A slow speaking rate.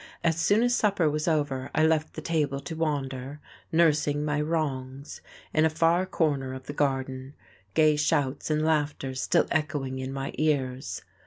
No: average, 165 wpm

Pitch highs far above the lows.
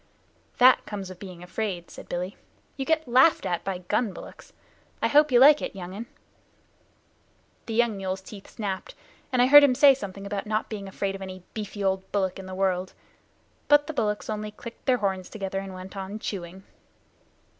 No: average, 3.9 semitones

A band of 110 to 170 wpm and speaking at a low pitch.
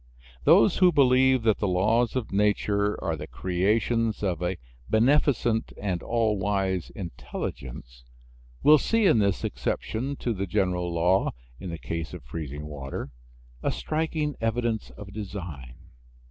Yes: average, 140 wpm; low, 105 Hz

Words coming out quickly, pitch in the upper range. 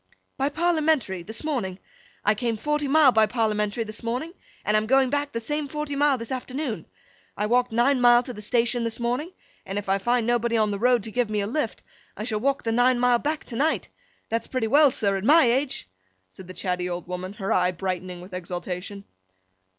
Yes: fast, 210 wpm; high, 235 Hz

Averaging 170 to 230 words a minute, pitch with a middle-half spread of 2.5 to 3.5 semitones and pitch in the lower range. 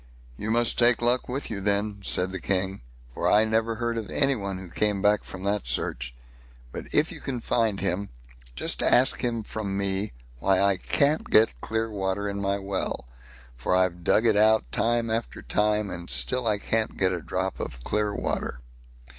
Yes: average, 190 wpm; average, 2.8 semitones; low, 105 Hz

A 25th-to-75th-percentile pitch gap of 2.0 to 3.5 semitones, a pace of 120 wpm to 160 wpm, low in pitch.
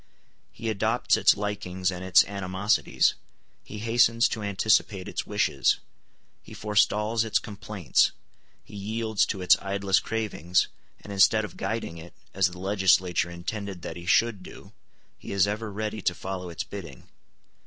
Yes: average, 2.9 semitones; average, 150 wpm; low, 100 Hz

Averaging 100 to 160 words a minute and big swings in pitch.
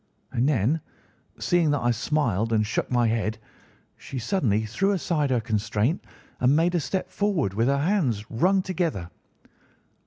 Yes: average, 155 wpm; wide, 7.3 semitones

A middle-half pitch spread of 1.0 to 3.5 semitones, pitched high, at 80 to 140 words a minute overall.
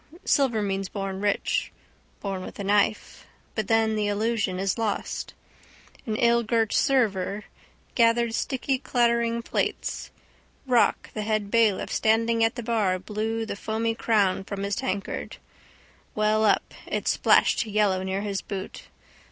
Yes: narrow, 2.4 semitones; high, 215 Hz; slow, 135 wpm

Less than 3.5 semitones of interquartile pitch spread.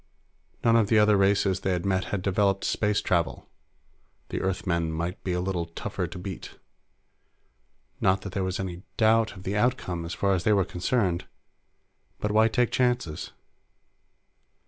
Yes: average, 2.8 semitones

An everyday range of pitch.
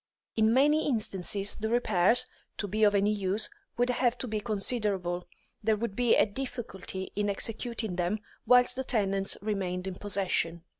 Yes: average, 3.5 semitones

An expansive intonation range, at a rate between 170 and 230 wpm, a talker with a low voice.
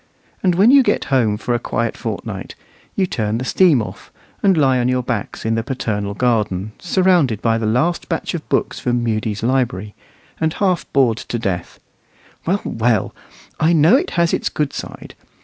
Yes: wide, 7.0 semitones; average, 185 wpm; low, 125 Hz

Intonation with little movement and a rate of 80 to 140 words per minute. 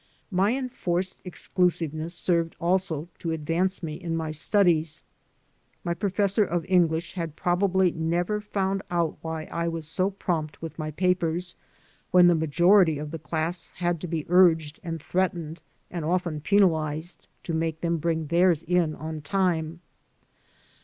No: narrow, 2.2 semitones; average, 150 wpm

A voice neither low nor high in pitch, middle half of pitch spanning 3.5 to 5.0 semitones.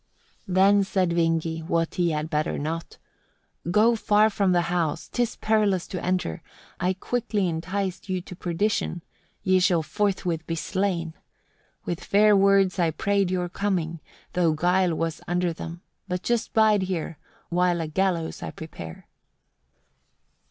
No: medium, 180 Hz; average, 3.0 semitones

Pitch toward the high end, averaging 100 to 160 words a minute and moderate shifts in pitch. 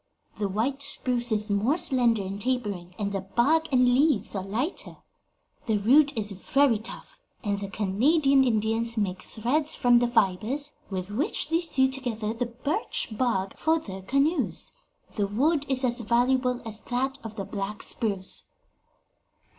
Yes: high, 235 Hz; average, 155 wpm; average, 4.7 semitones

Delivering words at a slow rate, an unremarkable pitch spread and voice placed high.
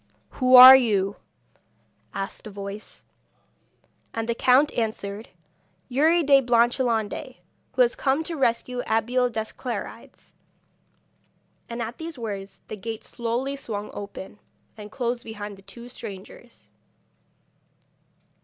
Yes: slow, 115 wpm; average, 3.3 semitones; high, 235 Hz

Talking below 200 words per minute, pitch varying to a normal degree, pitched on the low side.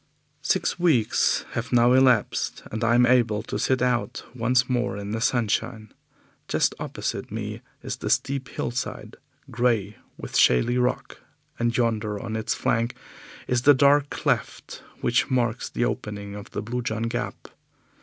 No: average, 155 wpm; narrow, 2.3 semitones; low, 120 Hz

